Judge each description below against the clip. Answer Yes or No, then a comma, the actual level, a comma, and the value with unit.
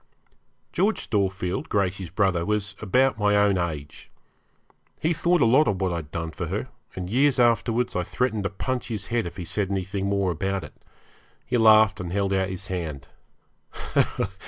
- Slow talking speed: No, average, 175 wpm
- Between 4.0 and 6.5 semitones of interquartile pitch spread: No, average, 3.6 semitones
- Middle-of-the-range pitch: No, low, 100 Hz